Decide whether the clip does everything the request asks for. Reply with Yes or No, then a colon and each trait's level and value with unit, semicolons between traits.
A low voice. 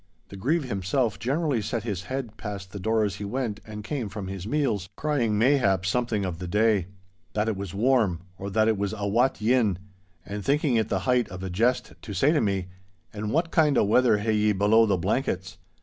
Yes: low, 105 Hz